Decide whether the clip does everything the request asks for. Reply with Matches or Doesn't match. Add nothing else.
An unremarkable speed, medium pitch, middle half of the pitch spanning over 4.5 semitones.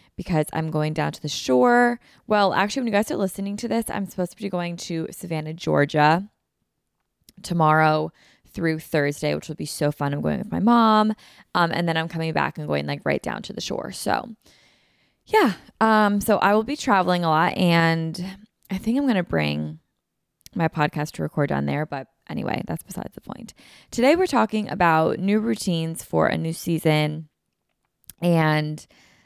Matches